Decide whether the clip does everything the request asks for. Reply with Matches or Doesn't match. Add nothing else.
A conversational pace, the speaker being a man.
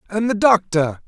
Matches